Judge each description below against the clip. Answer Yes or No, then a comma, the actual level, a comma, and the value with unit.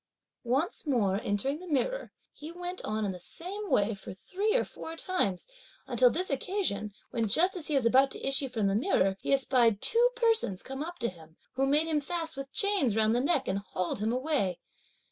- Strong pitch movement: Yes, wide, 8.7 semitones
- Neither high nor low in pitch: No, very high, 270 Hz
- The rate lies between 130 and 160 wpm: No, fast, 205 wpm